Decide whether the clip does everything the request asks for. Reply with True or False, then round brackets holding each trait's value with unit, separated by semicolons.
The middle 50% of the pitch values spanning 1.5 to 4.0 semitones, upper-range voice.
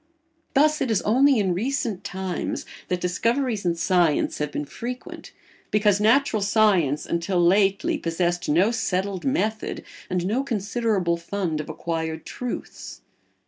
False (4.7 semitones; 200 Hz)